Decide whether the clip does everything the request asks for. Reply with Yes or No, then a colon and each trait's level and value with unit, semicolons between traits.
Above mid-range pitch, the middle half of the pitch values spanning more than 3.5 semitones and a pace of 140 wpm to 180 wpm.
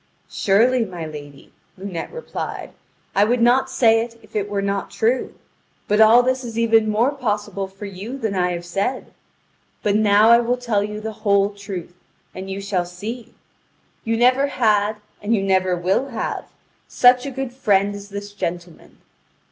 No: high, 210 Hz; average, 3.2 semitones; average, 170 wpm